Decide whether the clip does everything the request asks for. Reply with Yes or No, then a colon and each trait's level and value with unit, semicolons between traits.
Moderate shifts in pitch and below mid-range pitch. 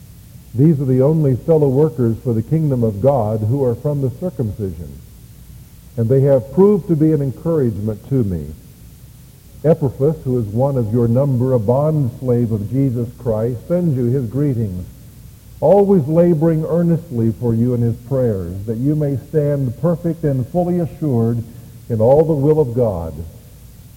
Yes: average, 4.5 semitones; low, 130 Hz